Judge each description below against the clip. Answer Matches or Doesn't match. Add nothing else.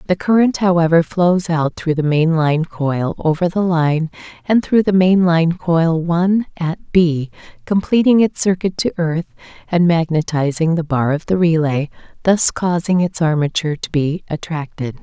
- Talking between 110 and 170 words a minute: Matches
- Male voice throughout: Doesn't match